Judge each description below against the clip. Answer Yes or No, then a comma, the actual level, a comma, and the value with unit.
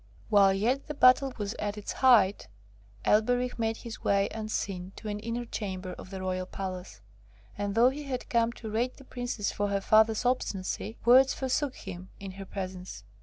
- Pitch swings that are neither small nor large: Yes, average, 4.0 semitones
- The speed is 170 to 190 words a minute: Yes, average, 180 wpm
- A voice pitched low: No, high, 215 Hz